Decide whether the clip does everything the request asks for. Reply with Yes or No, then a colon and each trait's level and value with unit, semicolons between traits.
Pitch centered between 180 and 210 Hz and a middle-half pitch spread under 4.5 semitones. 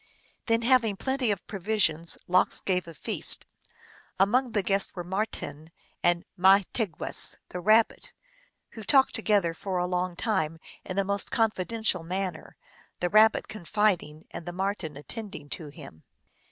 Yes: high, 190 Hz; average, 3.9 semitones